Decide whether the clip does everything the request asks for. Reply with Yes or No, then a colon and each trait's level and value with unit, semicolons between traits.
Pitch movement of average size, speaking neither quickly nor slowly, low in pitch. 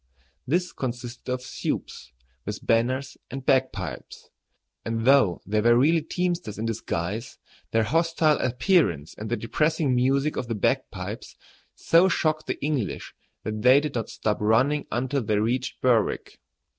Yes: average, 4.5 semitones; average, 145 wpm; low, 125 Hz